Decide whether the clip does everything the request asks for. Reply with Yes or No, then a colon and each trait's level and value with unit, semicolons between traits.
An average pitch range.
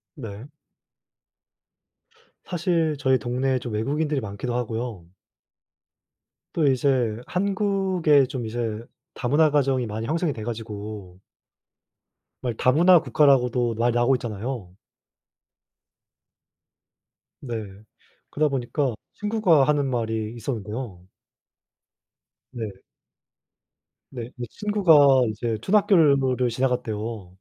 Yes: average, 4.7 semitones